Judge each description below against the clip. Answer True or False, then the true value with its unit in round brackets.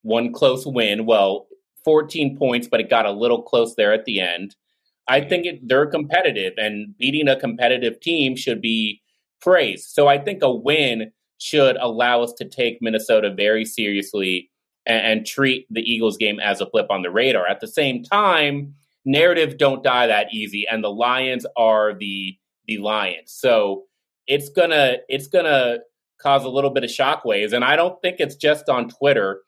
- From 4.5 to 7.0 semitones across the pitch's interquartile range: True (5.0 semitones)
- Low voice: True (130 Hz)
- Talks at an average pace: True (180 wpm)